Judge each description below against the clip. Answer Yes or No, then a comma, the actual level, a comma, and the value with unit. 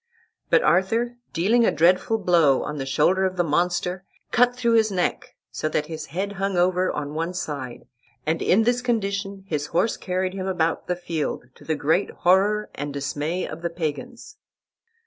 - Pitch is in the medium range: Yes, medium, 180 Hz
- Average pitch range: Yes, average, 4.1 semitones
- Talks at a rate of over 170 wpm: Yes, average, 180 wpm